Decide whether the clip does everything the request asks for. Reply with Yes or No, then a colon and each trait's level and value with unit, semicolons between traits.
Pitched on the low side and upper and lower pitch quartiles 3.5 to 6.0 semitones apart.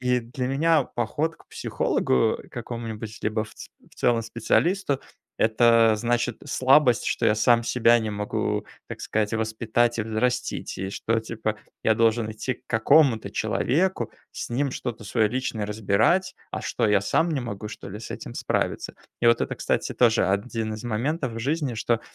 No: low, 115 Hz; narrow, 2.5 semitones